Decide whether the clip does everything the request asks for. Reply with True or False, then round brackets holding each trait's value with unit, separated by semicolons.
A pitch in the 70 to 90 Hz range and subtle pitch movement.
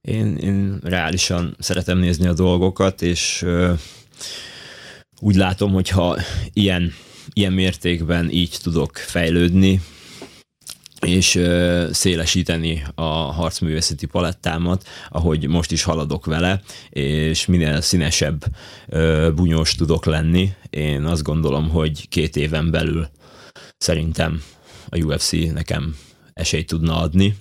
True (85 Hz; 2.3 semitones)